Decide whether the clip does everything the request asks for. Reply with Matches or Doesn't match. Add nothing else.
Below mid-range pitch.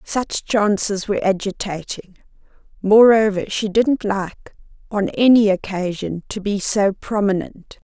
Doesn't match